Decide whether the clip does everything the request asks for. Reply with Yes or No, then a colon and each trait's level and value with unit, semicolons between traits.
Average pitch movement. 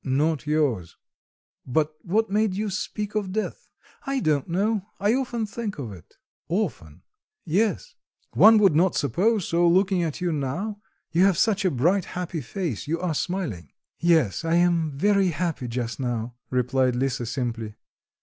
No: wide, 6.8 semitones